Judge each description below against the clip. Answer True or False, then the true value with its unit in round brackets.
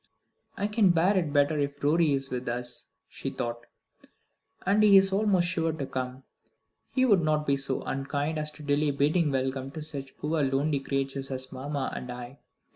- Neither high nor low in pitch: True (145 Hz)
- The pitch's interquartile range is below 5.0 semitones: True (3.3 semitones)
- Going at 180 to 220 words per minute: True (185 wpm)